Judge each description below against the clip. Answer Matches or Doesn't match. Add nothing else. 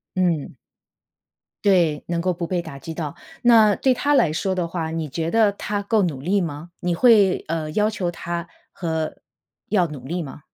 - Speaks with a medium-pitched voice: Matches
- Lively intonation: Doesn't match